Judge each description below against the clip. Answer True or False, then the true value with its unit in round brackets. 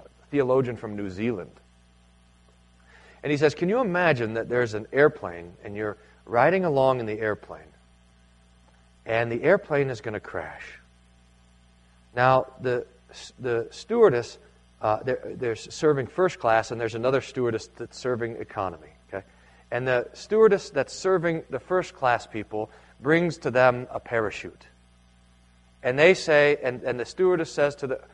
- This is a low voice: True (115 Hz)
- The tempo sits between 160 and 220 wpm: False (150 wpm)